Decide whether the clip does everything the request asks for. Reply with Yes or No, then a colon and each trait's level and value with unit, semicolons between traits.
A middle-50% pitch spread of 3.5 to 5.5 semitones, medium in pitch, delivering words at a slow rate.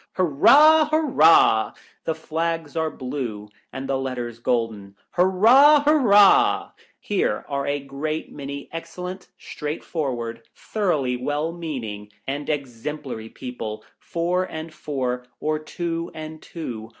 Yes: average, 5.1 semitones; medium, 150 Hz; slow, 120 wpm